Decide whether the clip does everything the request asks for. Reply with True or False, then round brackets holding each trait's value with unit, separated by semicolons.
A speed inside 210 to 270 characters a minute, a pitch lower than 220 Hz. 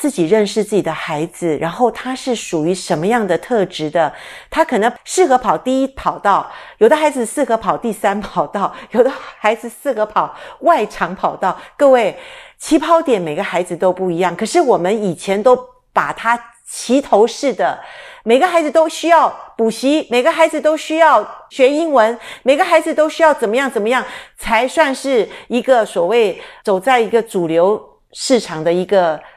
False (265 characters per minute; 245 Hz)